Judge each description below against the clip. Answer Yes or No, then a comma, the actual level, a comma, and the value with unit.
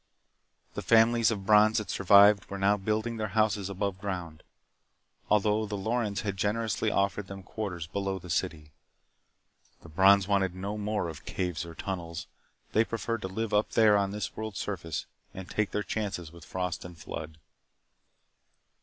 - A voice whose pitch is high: No, low, 100 Hz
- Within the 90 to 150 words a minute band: No, average, 165 wpm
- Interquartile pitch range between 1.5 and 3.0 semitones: Yes, average, 2.7 semitones